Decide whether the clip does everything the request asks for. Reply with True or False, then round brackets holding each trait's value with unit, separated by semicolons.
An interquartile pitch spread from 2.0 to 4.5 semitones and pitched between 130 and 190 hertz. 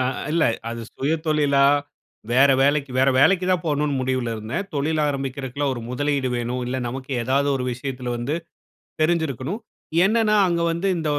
True (3.5 semitones; 140 Hz)